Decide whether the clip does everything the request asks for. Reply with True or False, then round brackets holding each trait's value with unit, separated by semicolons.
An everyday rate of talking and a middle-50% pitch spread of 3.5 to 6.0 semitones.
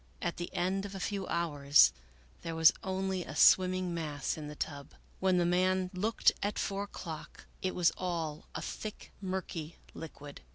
False (170 wpm; 2.9 semitones)